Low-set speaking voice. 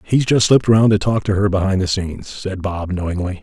Yes: low, 100 Hz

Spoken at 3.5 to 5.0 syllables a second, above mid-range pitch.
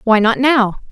Yes: 4.1 syllables/s; high, 235 Hz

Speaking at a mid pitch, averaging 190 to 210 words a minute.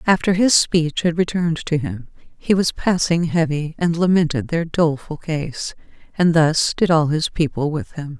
No: medium, 160 Hz; average, 175 wpm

